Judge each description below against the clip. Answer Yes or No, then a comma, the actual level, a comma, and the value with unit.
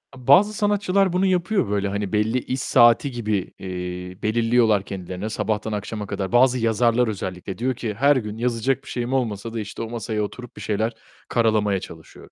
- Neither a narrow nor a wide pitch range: Yes, average, 3.4 semitones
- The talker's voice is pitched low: Yes, low, 115 Hz